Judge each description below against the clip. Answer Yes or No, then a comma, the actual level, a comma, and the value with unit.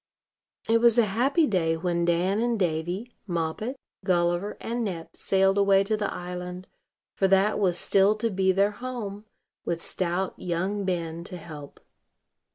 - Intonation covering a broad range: No, average, 3.3 semitones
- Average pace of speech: Yes, average, 155 wpm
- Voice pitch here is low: No, high, 190 Hz